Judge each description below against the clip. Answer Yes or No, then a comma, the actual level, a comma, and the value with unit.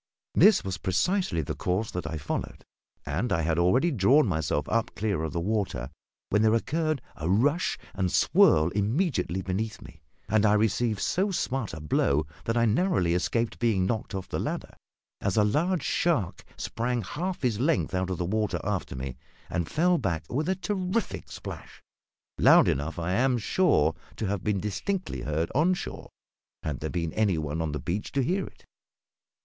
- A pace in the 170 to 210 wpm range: Yes, average, 180 wpm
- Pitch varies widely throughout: Yes, wide, 7.6 semitones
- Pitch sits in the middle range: No, low, 105 Hz